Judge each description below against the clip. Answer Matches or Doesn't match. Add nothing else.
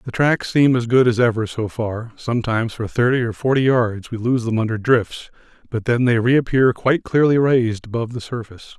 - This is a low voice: Matches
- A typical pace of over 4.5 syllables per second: Matches